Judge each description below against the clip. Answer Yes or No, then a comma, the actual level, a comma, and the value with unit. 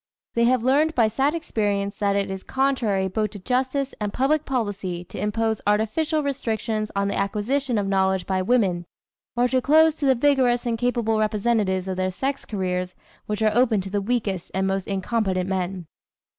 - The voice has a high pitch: Yes, high, 215 Hz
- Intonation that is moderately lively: Yes, average, 4.6 semitones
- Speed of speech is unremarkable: Yes, average, 185 wpm